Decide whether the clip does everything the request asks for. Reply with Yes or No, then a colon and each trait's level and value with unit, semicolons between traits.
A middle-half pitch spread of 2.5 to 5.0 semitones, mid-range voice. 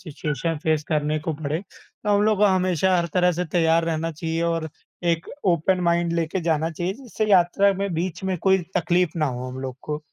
Yes: average, 3.0 semitones; medium, 170 Hz